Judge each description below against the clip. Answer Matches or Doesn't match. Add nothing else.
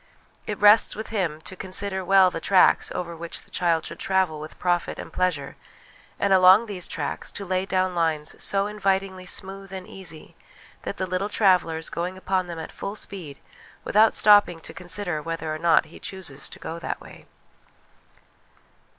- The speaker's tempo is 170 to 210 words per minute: Matches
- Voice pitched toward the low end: Doesn't match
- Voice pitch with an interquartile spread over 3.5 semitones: Doesn't match